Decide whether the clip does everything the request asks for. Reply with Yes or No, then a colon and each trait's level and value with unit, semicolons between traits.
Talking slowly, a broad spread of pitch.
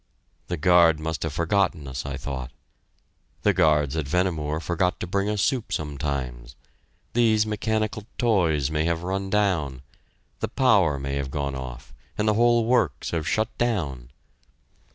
No: average, 155 wpm; wide, 6.7 semitones